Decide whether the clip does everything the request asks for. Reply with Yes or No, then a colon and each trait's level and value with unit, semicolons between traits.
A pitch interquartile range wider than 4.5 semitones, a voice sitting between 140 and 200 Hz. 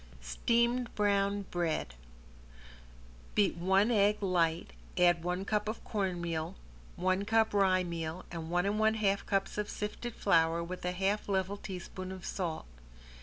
No: average, 2.9 semitones; high, 190 Hz